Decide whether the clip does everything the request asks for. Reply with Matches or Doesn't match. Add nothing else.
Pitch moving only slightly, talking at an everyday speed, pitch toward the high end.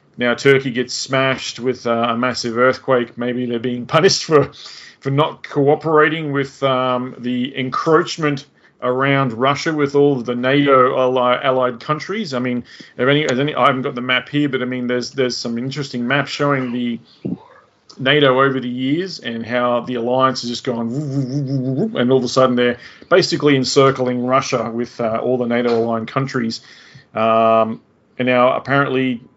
Doesn't match